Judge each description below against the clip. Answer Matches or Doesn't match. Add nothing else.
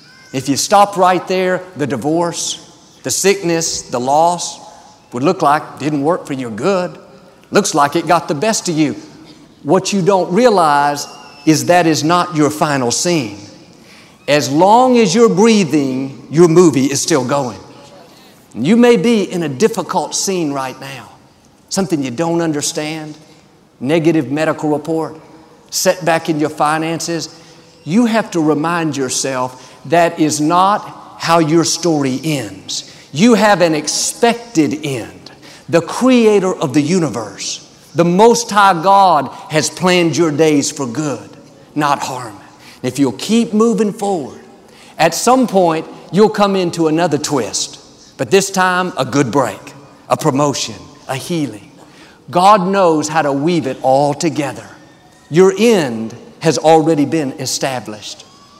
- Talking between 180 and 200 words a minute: Doesn't match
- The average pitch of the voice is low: Doesn't match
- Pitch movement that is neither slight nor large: Matches